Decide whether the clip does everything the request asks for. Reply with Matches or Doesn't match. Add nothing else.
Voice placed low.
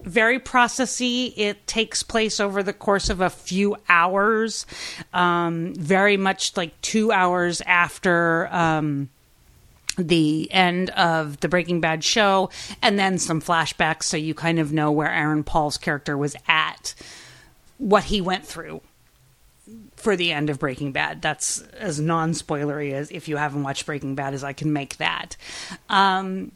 Doesn't match